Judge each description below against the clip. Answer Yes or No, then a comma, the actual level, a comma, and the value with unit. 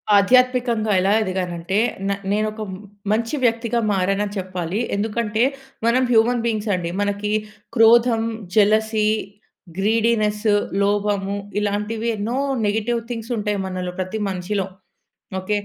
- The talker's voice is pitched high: Yes, high, 210 Hz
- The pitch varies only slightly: Yes, narrow, 2.3 semitones